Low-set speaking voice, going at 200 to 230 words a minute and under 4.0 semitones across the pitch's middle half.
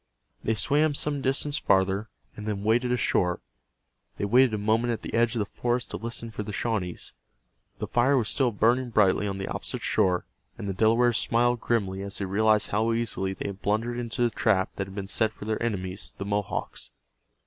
Yes: low, 110 Hz; fast, 205 wpm; average, 3.3 semitones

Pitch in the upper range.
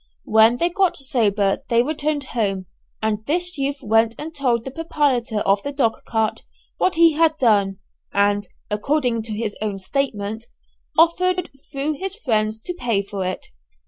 Yes: high, 240 Hz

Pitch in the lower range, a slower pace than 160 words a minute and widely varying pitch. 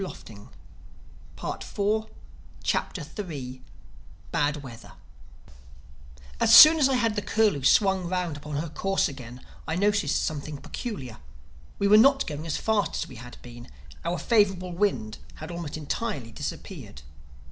No: medium, 170 Hz; slow, 135 wpm; wide, 6.6 semitones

